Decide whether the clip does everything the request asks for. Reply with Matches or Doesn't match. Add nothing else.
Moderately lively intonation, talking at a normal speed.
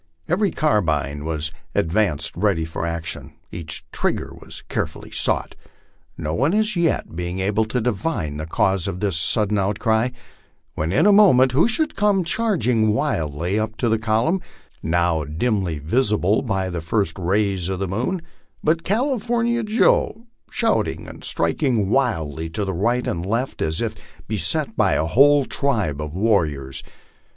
Doesn't match